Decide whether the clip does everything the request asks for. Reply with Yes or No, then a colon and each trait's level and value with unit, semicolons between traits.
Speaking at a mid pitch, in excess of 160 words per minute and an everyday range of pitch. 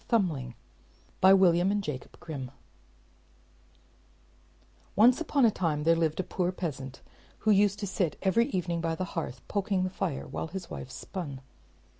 No: medium, 180 Hz; average, 155 wpm; average, 4.1 semitones